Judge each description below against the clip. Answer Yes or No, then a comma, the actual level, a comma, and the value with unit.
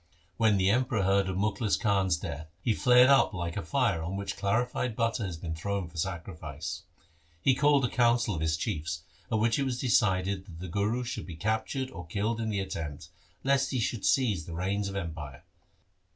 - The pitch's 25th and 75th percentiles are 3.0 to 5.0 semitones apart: No, wide, 5.4 semitones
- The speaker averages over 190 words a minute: Yes, average, 200 wpm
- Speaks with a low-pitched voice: Yes, low, 100 Hz